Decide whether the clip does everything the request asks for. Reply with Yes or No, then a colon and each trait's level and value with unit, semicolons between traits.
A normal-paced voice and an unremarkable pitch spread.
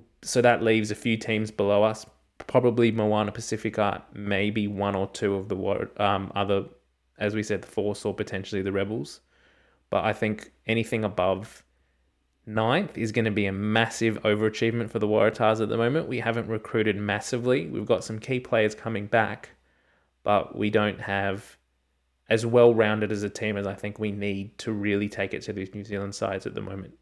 No: average, 185 wpm; narrow, 2.0 semitones